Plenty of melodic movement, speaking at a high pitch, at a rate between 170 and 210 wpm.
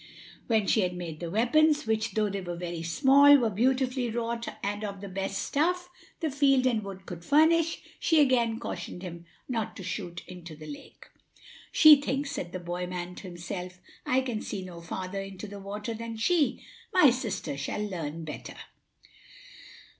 Yes: wide, 6.3 semitones; high, 210 Hz; average, 175 wpm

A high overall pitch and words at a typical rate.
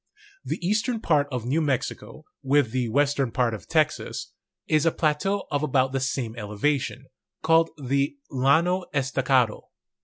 No: medium, 140 Hz; average, 145 wpm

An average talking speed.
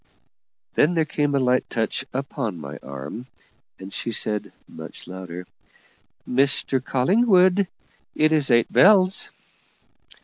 No: slow, 115 wpm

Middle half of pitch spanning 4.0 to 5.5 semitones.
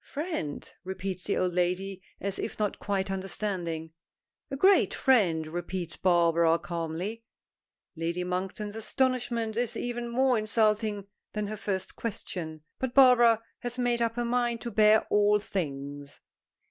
Yes: average, 4.9 semitones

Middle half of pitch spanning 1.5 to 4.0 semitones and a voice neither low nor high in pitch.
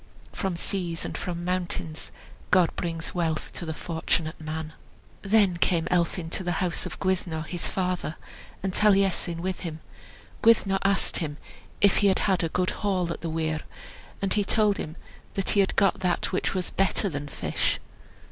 Yes: average, 2.9 semitones; medium, 180 Hz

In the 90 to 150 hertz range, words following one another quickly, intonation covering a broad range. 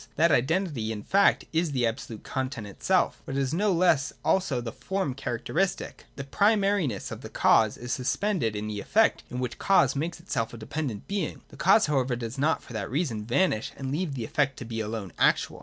Yes: low, 135 Hz; fast, 210 wpm; wide, 6.7 semitones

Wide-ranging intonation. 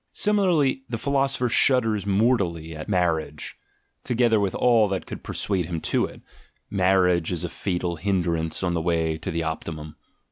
Yes: wide, 5.7 semitones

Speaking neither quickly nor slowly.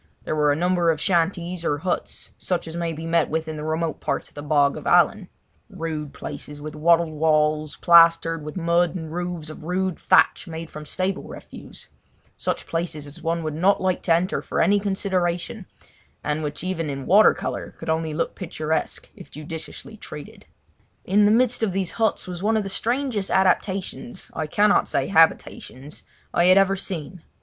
Yes: average, 175 wpm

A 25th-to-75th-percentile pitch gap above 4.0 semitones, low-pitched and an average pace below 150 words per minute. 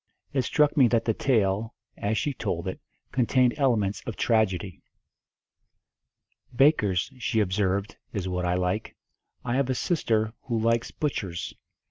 Yes: average, 4.7 semitones; low, 110 Hz; average, 140 wpm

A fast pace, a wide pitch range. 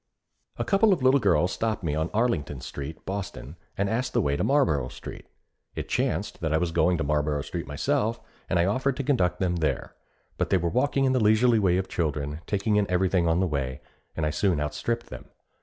Yes: fast, 215 wpm; wide, 6.8 semitones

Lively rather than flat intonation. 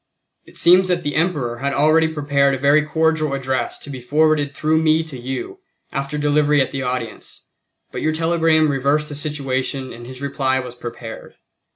No: average, 3.0 semitones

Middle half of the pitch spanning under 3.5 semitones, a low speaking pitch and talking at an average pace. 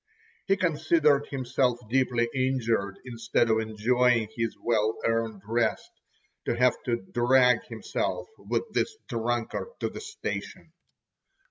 No: narrow, 2.6 semitones; low, 120 Hz; slow, 120 wpm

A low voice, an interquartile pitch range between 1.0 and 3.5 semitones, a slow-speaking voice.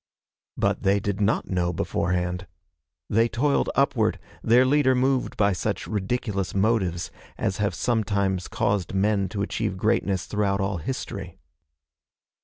Yes: low, 100 Hz; average, 3.1 semitones; slow, 130 wpm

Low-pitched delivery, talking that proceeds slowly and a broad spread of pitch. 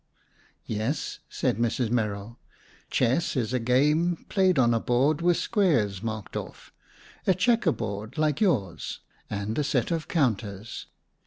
Yes: low, 125 Hz; slow, 130 wpm; wide, 6.8 semitones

